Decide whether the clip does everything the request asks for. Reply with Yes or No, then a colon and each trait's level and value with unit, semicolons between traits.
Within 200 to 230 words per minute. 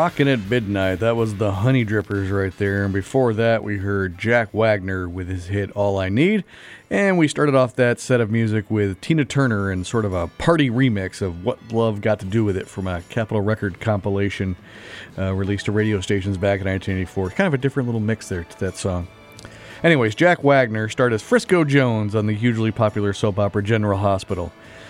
Yes: fast, 205 wpm